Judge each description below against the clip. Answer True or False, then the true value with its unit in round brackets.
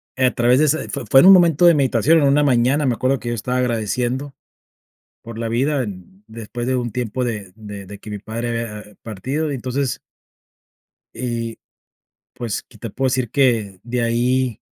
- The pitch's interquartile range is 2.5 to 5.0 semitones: True (2.9 semitones)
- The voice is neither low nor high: False (120 Hz)